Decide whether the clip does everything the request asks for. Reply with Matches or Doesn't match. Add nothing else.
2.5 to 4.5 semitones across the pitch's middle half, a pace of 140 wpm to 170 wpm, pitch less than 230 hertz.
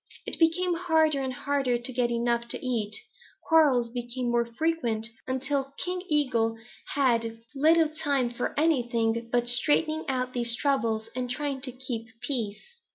Doesn't match